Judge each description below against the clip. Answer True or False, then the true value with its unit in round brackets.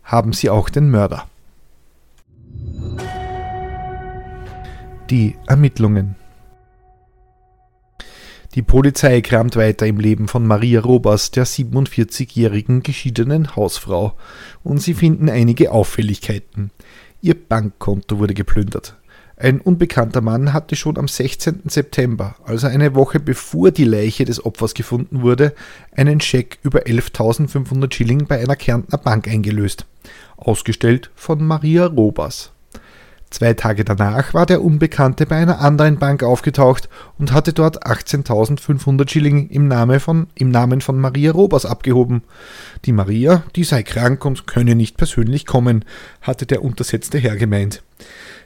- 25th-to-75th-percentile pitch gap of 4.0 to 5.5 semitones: True (4.6 semitones)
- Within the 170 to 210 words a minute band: False (125 wpm)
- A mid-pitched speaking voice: False (125 Hz)